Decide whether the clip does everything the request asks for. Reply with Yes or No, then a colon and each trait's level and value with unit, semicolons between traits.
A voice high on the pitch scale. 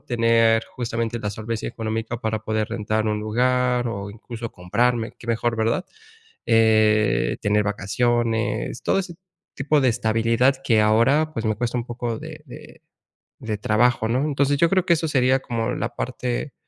No: low, 115 Hz